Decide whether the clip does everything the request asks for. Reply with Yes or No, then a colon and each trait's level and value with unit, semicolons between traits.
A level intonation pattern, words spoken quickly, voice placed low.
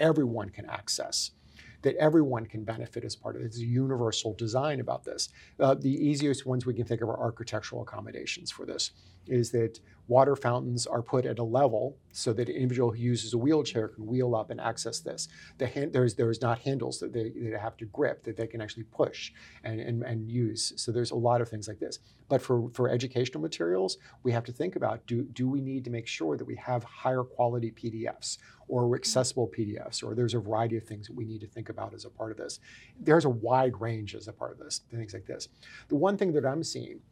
Yes: narrow, 2.2 semitones; fast, 230 wpm; low, 120 Hz